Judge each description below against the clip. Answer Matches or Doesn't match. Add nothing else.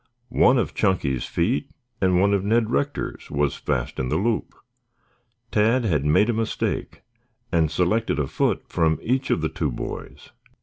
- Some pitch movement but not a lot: Doesn't match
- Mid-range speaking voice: Doesn't match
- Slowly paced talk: Doesn't match